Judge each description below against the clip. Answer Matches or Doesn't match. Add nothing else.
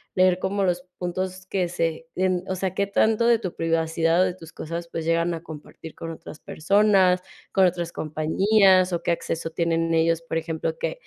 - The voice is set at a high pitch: Doesn't match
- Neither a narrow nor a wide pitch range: Doesn't match